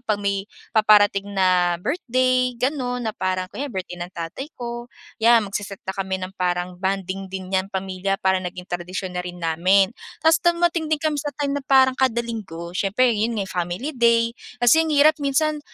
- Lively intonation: Yes, wide, 5.7 semitones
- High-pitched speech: Yes, high, 205 Hz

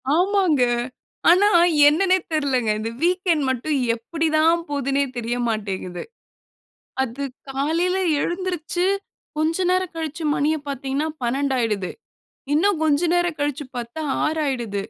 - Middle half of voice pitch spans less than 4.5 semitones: No, average, 4.8 semitones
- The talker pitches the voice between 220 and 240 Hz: No, very high, 300 Hz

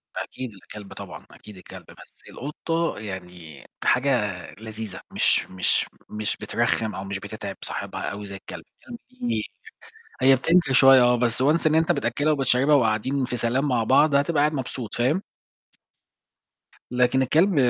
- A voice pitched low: Yes, low, 125 Hz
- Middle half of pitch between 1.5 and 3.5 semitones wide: No, average, 5.3 semitones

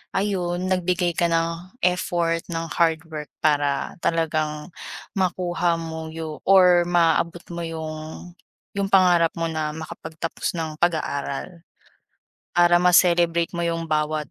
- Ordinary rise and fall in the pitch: No, narrow, 1.7 semitones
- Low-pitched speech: No, medium, 170 Hz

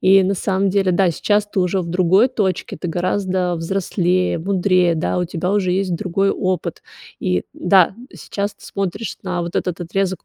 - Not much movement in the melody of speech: Yes, narrow, 1.8 semitones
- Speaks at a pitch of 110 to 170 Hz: No, medium, 185 Hz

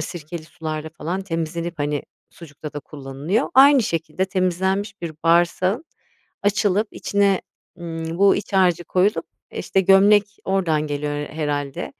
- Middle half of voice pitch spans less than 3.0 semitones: No, average, 3.9 semitones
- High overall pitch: No, medium, 170 Hz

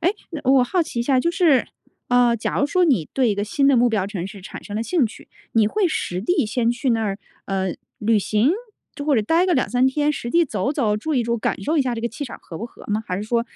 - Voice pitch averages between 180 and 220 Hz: No, high, 240 Hz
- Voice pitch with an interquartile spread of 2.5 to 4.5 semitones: No, average, 5.2 semitones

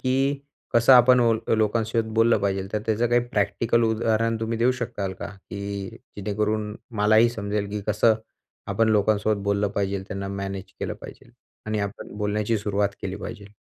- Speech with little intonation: Yes, narrow, 2.1 semitones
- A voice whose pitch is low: Yes, low, 105 Hz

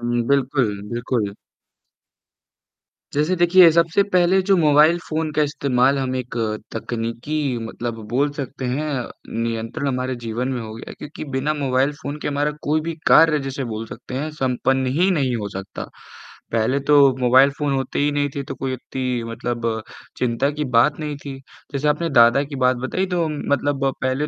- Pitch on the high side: No, low, 135 Hz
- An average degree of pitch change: Yes, average, 3.4 semitones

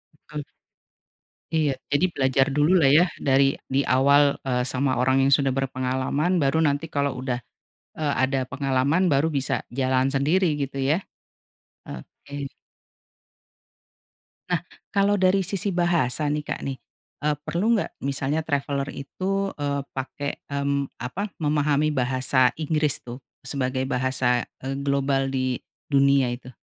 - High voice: No, medium, 140 Hz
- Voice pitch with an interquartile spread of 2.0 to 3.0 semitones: Yes, narrow, 2.4 semitones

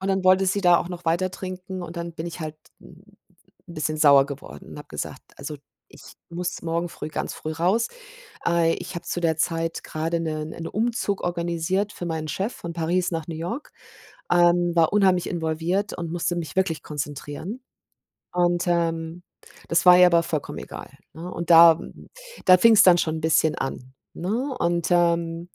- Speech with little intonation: Yes, narrow, 2.0 semitones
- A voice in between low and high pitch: Yes, medium, 170 Hz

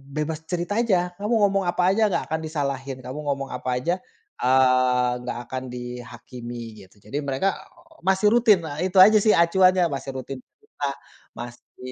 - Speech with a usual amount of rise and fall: No, wide, 6.6 semitones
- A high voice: No, medium, 140 Hz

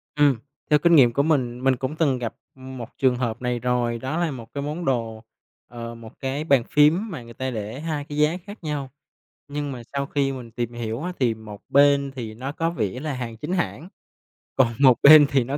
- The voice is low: Yes, low, 130 Hz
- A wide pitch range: No, average, 3.7 semitones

